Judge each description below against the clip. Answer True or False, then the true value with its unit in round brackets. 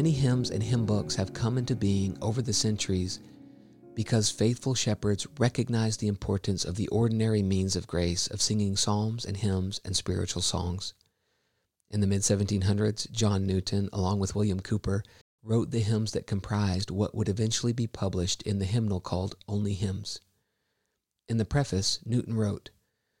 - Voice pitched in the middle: False (105 Hz)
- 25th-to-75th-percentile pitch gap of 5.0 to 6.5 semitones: False (2.4 semitones)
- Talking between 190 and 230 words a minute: False (165 wpm)